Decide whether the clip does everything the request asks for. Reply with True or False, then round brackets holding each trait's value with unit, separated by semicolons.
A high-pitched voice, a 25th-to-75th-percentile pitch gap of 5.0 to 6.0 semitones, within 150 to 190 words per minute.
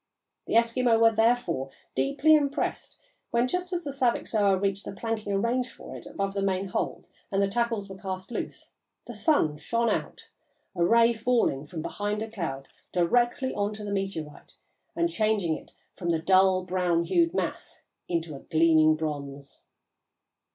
True (200 Hz; 5.5 semitones; 160 wpm)